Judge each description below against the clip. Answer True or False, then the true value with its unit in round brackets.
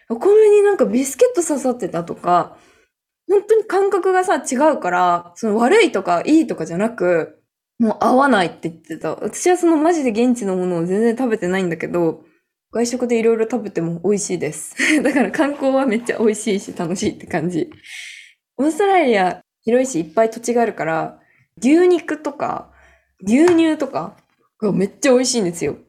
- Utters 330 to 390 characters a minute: True (370 characters per minute)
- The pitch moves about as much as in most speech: False (8.9 semitones)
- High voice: True (240 Hz)